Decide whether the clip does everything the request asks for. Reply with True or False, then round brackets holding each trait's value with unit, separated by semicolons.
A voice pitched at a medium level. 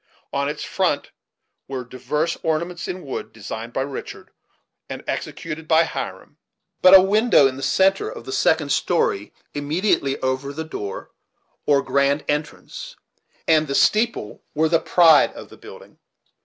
True (150 Hz)